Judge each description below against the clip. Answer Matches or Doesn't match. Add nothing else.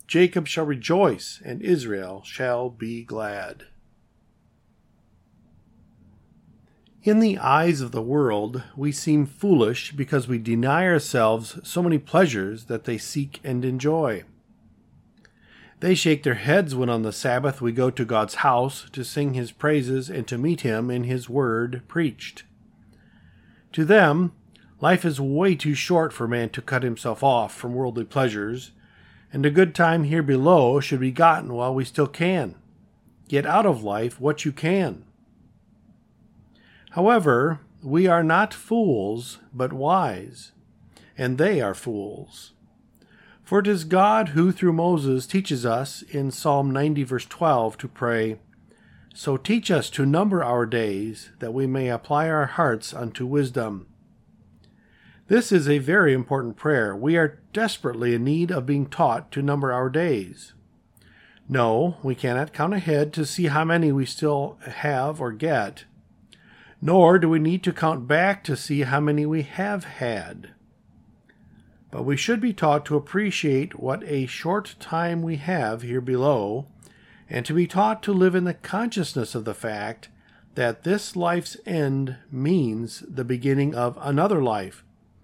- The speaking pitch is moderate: Matches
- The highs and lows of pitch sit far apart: Matches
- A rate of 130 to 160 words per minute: Matches